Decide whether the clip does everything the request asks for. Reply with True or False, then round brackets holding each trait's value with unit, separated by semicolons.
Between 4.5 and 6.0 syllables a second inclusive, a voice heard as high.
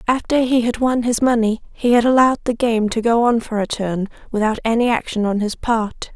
True (5.4 syllables/s; 230 Hz)